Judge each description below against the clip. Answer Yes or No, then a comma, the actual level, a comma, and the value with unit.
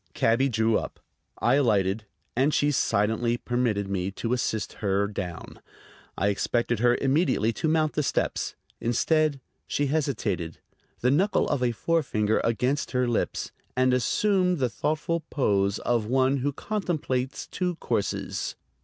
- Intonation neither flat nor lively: Yes, average, 4.9 semitones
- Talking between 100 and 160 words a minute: Yes, average, 140 wpm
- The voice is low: Yes, low, 125 Hz